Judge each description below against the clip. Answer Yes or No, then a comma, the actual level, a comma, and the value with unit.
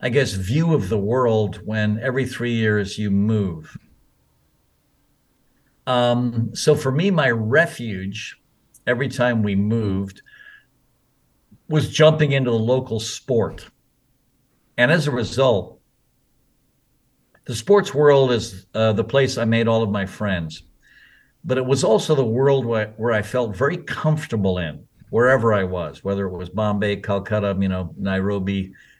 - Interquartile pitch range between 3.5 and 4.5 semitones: No, average, 5.0 semitones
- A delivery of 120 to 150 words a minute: Yes, average, 145 wpm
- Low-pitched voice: Yes, low, 115 Hz